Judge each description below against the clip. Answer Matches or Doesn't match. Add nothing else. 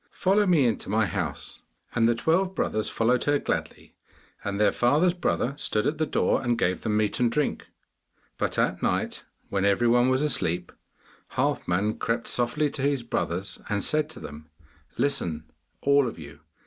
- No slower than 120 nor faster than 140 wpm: Doesn't match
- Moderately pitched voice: Doesn't match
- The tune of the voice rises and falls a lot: Matches